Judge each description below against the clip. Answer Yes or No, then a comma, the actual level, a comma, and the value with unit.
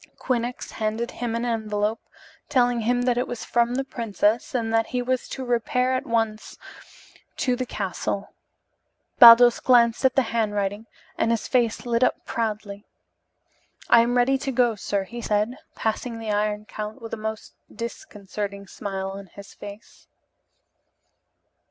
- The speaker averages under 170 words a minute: Yes, average, 150 wpm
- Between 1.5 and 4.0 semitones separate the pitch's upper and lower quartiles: Yes, narrow, 2.6 semitones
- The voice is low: No, high, 230 Hz